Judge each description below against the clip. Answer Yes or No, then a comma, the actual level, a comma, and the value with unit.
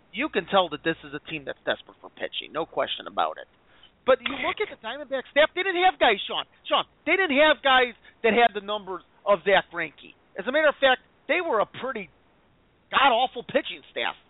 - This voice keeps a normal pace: No, fast, 225 wpm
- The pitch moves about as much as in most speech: No, wide, 7.8 semitones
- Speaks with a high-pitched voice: Yes, very high, 255 Hz